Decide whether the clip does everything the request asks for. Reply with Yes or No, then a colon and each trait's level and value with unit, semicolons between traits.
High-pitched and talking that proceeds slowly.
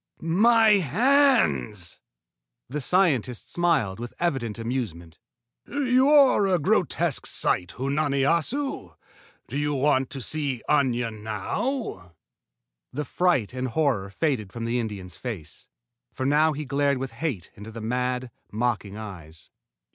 No: low, 130 Hz; slow, 125 wpm